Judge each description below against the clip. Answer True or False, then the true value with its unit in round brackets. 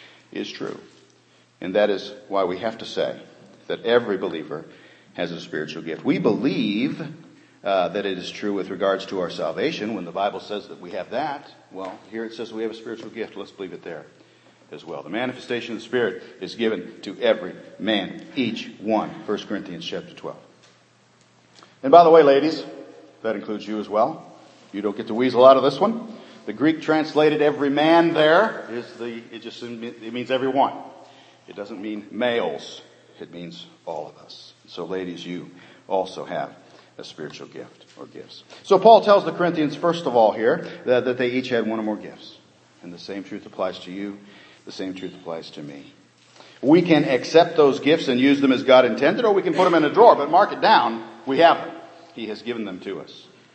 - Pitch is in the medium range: False (115 Hz)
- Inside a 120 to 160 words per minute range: False (205 wpm)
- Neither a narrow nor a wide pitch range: False (6.4 semitones)